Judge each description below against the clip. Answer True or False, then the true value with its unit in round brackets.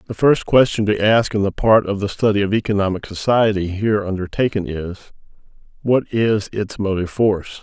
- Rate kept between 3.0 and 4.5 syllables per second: False (5.5 syllables/s)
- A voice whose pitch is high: False (105 Hz)